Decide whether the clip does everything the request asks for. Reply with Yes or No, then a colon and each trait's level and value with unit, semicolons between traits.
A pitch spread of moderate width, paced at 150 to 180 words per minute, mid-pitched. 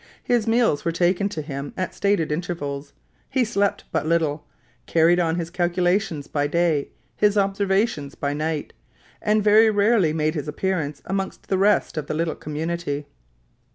Yes: average, 4.7 semitones; average, 155 wpm; medium, 170 Hz